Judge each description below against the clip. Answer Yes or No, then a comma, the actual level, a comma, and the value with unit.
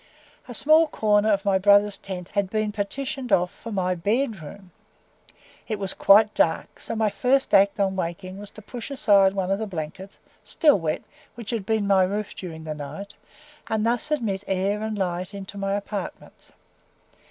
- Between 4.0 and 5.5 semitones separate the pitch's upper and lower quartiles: No, narrow, 2.4 semitones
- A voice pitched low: No, high, 200 Hz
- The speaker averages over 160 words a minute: Yes, average, 180 wpm